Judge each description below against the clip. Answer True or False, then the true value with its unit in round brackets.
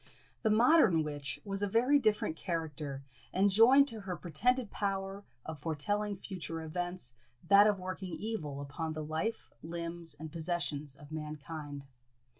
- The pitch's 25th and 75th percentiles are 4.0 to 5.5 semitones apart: True (4.8 semitones)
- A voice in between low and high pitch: True (175 Hz)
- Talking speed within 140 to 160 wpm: True (145 wpm)